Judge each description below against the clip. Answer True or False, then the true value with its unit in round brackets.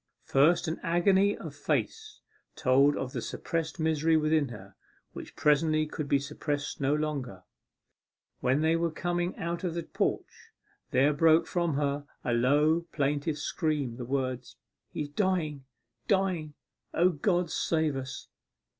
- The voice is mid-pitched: True (155 Hz)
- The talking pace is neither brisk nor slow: True (145 wpm)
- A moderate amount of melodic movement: True (3.2 semitones)